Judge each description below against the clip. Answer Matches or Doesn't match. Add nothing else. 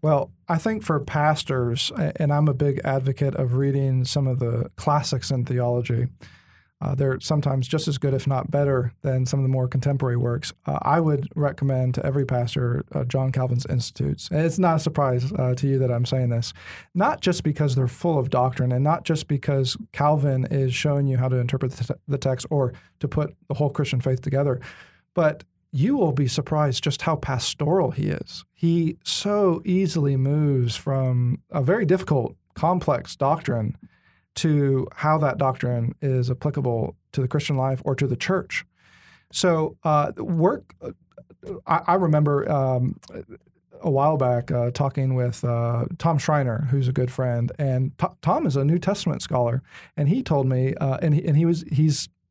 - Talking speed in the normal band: Matches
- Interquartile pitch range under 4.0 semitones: Matches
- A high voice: Doesn't match